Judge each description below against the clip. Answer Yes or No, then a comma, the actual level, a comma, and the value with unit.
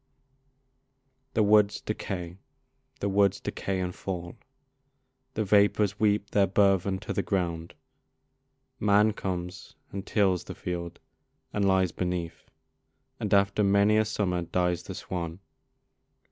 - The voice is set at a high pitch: No, low, 100 Hz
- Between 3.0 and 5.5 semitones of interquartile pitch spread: No, narrow, 2.5 semitones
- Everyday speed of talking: No, slow, 125 wpm